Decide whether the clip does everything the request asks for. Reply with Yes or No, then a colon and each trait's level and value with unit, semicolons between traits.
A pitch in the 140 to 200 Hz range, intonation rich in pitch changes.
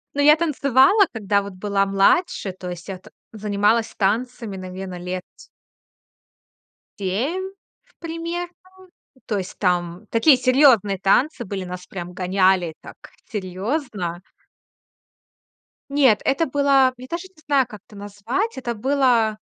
No: high, 215 Hz; wide, 6.3 semitones